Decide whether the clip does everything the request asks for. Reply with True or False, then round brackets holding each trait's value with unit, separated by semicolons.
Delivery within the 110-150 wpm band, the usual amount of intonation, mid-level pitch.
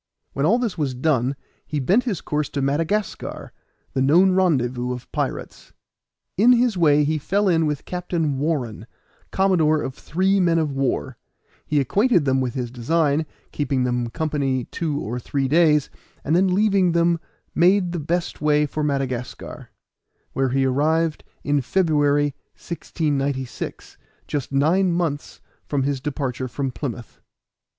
True (145 wpm; 4.2 semitones; 150 Hz)